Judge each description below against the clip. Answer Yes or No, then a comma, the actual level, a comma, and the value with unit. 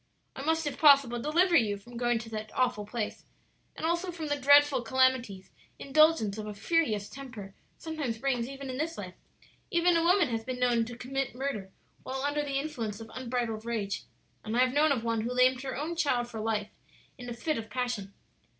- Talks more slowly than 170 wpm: No, fast, 205 wpm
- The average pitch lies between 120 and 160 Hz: No, very high, 250 Hz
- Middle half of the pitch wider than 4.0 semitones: Yes, average, 4.4 semitones